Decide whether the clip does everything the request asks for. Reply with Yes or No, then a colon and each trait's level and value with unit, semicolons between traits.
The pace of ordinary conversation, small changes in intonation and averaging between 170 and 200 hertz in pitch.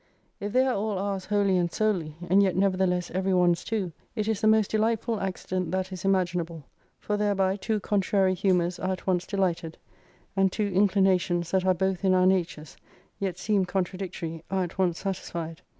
Yes: average, 185 wpm; narrow, 1.9 semitones; high, 190 Hz